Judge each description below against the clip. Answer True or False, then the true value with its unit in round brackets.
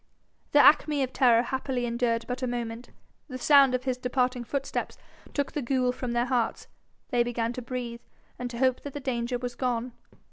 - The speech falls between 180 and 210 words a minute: True (190 wpm)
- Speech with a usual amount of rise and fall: False (1.6 semitones)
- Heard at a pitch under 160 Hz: False (250 Hz)